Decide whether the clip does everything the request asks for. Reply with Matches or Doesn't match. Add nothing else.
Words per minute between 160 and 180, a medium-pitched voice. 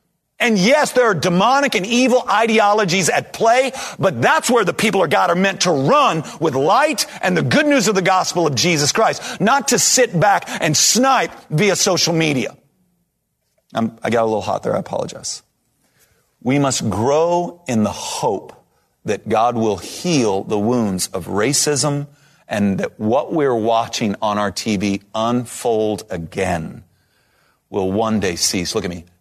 Matches